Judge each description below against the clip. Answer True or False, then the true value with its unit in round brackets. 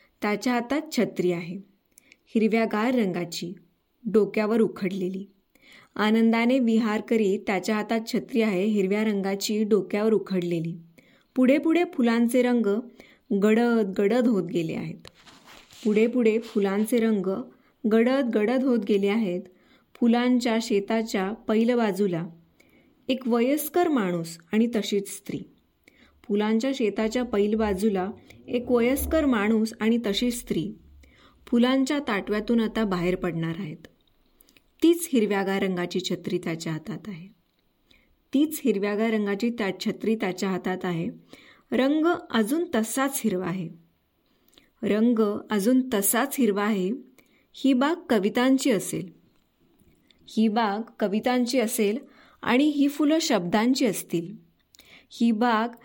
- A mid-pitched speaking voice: False (220 Hz)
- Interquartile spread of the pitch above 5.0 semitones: False (3.8 semitones)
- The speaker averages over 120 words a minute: False (110 wpm)